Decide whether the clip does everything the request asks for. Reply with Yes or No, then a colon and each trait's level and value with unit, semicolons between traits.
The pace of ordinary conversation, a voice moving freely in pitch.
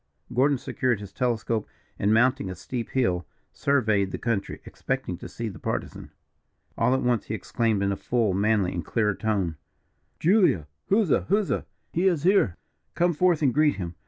Yes: average, 170 wpm; wide, 6.1 semitones